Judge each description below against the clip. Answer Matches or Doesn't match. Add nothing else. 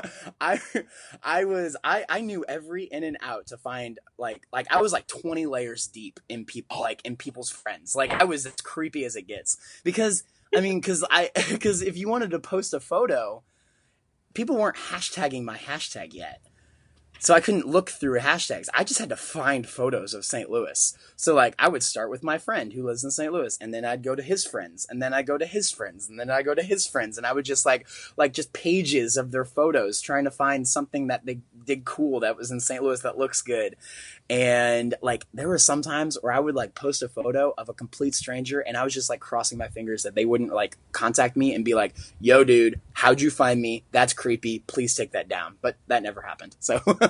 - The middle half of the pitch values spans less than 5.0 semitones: Doesn't match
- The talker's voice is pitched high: Doesn't match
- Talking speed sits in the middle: Doesn't match